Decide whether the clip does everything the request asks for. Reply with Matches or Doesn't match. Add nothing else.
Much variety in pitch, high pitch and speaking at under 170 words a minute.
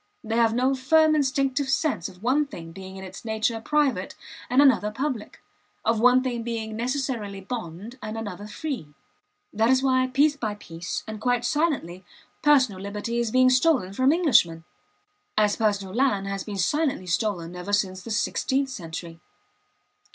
Doesn't match